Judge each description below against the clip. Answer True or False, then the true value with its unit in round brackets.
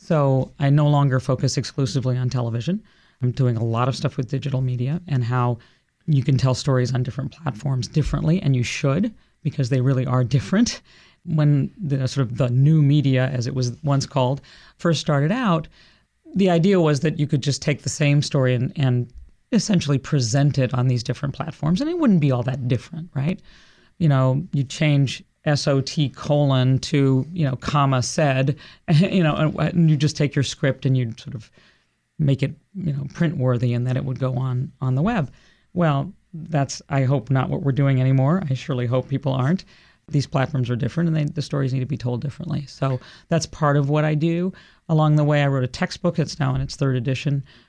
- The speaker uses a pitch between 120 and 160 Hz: True (140 Hz)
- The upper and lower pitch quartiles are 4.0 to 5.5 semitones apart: False (3.0 semitones)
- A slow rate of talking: False (205 wpm)